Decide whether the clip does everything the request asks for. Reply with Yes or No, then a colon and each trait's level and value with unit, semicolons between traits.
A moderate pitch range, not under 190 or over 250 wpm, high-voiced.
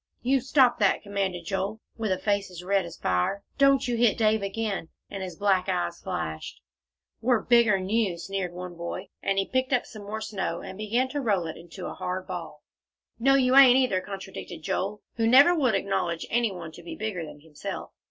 Yes: average, 4.3 semitones; average, 200 wpm; high, 200 Hz